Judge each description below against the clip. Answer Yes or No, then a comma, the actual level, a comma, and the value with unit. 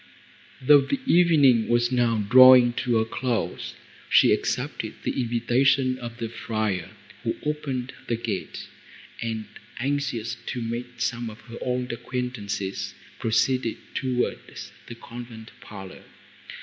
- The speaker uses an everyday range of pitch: No, narrow, 2.1 semitones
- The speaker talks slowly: Yes, slow, 125 wpm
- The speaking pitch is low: Yes, low, 120 Hz